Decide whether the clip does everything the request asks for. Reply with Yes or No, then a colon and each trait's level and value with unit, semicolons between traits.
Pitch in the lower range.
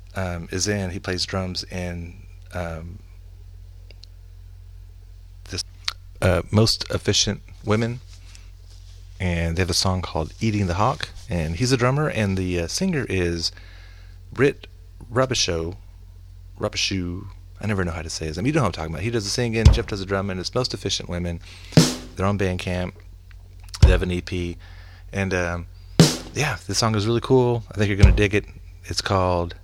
Yes: very low, 90 Hz